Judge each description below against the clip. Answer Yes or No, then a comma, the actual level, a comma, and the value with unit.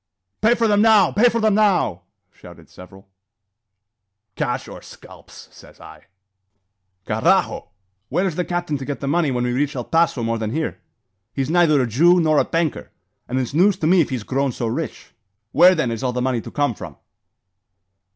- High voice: No, medium, 150 Hz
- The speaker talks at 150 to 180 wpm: No, average, 190 wpm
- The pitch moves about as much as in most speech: No, wide, 6.1 semitones